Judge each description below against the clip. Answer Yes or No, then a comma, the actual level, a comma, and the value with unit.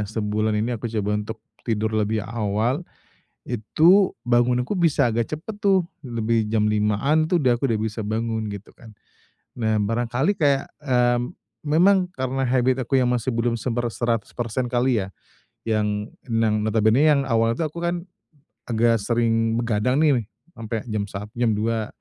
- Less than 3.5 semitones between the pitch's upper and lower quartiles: Yes, average, 2.9 semitones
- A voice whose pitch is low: Yes, low, 115 Hz